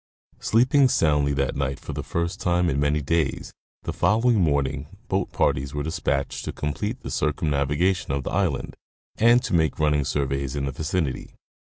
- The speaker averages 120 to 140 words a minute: No, average, 170 wpm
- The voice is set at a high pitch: No, very low, 75 Hz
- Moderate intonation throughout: Yes, average, 4.4 semitones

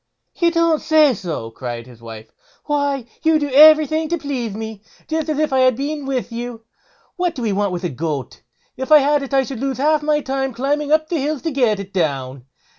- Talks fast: Yes, fast, 225 wpm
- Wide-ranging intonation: Yes, wide, 6.8 semitones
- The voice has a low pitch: No, very high, 270 Hz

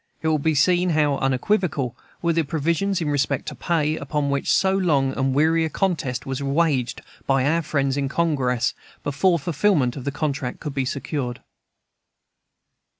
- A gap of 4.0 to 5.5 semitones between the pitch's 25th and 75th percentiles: No, average, 3.4 semitones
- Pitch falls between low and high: Yes, medium, 145 Hz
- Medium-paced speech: Yes, average, 170 wpm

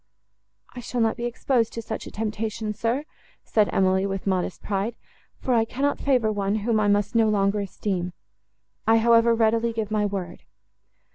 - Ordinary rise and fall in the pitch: No, narrow, 2.3 semitones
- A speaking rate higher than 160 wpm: Yes, average, 170 wpm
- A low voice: No, high, 220 Hz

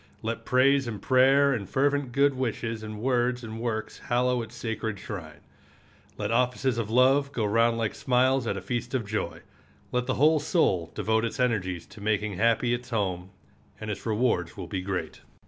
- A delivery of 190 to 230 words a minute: No, average, 180 wpm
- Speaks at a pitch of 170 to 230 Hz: No, low, 115 Hz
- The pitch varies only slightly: No, average, 3.2 semitones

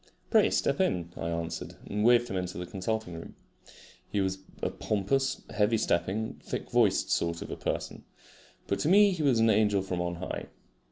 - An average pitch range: Yes, average, 4.4 semitones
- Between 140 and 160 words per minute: No, average, 180 wpm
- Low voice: Yes, low, 100 Hz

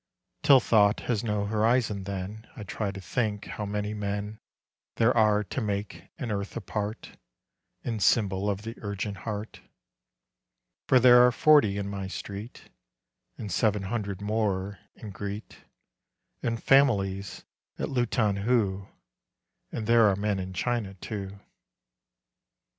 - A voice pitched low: Yes, low, 105 Hz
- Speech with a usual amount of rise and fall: No, narrow, 2.3 semitones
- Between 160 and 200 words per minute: No, slow, 135 wpm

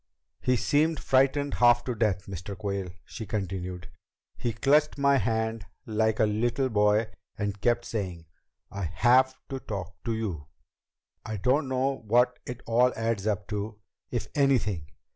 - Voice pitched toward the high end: No, low, 110 Hz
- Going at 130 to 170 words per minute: Yes, average, 150 wpm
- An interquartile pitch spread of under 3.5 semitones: No, average, 3.9 semitones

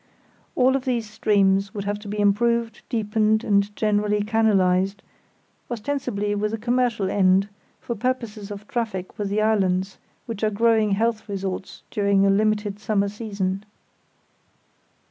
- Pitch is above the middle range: Yes, high, 210 Hz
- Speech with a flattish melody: Yes, narrow, 2.1 semitones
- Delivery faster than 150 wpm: No, average, 140 wpm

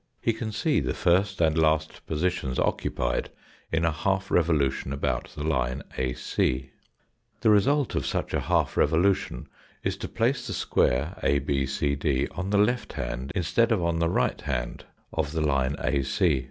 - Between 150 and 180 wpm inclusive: Yes, average, 165 wpm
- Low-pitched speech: Yes, very low, 80 Hz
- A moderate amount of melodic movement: No, wide, 6.0 semitones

